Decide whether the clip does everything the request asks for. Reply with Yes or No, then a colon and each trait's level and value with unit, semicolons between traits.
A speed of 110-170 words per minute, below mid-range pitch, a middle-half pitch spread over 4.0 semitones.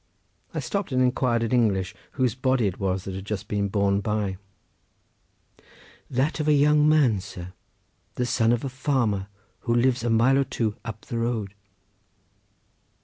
Yes: average, 165 wpm; low, 115 Hz; average, 4.4 semitones